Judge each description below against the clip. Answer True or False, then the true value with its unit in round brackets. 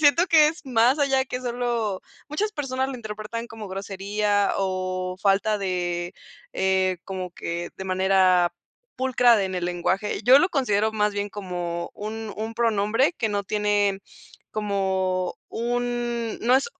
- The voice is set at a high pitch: True (210 Hz)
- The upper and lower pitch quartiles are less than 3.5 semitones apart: False (4.2 semitones)